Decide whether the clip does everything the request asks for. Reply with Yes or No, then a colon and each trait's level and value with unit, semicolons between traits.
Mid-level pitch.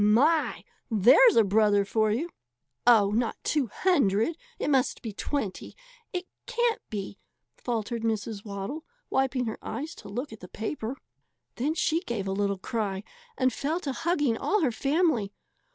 No: high, 235 Hz